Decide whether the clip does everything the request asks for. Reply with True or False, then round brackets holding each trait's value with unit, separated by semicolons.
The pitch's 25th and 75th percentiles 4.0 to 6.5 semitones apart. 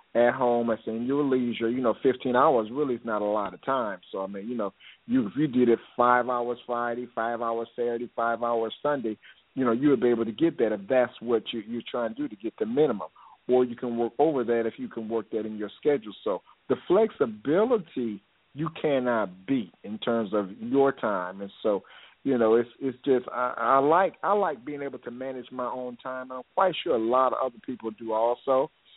False (2.7 semitones)